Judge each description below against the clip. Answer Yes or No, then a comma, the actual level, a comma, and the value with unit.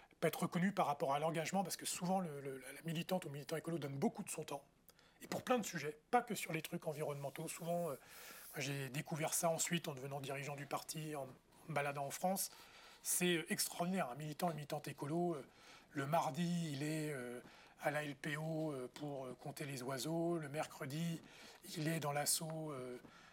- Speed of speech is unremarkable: Yes, average, 210 wpm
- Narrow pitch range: No, average, 3.0 semitones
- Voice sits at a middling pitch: Yes, medium, 155 Hz